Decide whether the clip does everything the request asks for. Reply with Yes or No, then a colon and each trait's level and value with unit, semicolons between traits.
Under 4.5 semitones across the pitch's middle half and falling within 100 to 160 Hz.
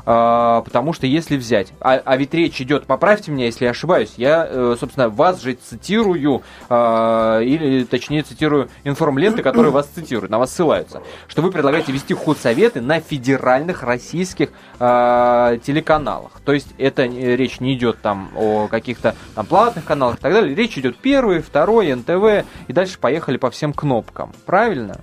No: average, 4.8 semitones; low, 135 Hz